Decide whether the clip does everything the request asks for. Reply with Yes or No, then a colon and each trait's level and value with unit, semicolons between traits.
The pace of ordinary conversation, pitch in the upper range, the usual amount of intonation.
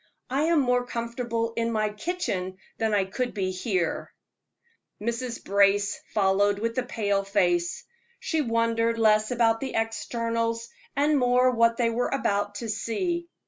Yes: average, 145 wpm; high, 230 Hz; average, 3.2 semitones